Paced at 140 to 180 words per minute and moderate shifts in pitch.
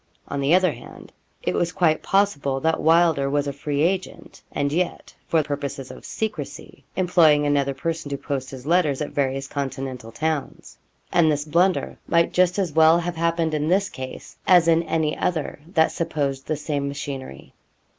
Yes: average, 175 wpm; average, 3.2 semitones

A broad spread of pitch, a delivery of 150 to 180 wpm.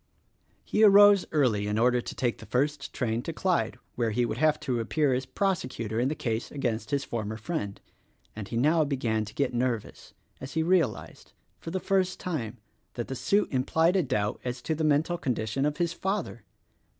No: wide, 5.7 semitones; average, 195 wpm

